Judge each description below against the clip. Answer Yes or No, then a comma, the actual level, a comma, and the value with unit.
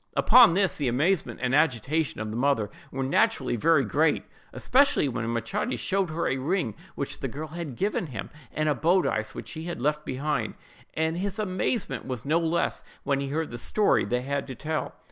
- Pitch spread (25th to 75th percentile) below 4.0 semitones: No, average, 4.8 semitones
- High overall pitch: No, medium, 150 Hz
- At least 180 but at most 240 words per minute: Yes, average, 200 wpm